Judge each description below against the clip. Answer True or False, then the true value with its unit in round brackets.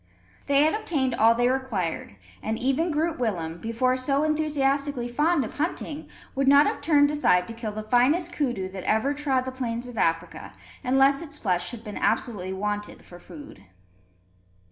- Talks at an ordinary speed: True (170 wpm)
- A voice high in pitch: True (255 Hz)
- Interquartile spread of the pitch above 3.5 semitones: True (5.1 semitones)